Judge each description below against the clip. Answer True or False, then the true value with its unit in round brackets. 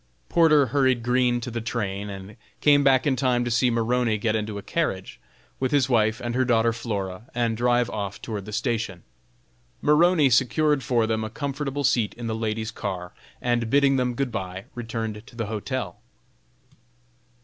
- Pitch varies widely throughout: False (3.0 semitones)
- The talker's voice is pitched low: True (120 Hz)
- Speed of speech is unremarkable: True (175 wpm)